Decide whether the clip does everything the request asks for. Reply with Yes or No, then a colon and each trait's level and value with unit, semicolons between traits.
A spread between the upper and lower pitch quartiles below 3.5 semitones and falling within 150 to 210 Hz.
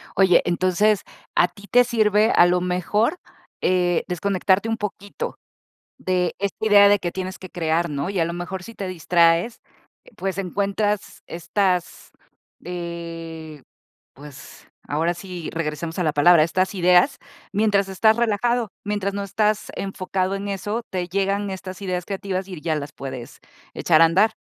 Yes: average, 2.8 semitones; medium, 185 Hz